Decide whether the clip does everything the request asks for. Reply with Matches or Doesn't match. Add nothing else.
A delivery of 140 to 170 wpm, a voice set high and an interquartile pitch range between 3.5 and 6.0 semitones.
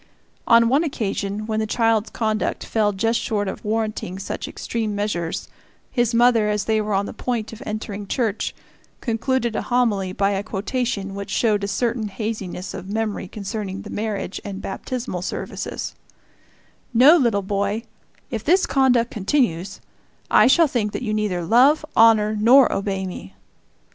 Doesn't match